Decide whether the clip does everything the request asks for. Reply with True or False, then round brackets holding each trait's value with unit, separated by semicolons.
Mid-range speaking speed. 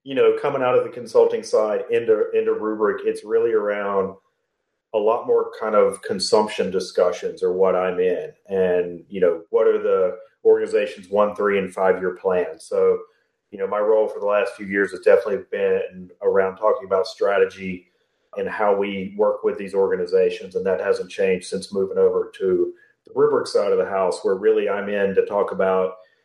True (190 wpm)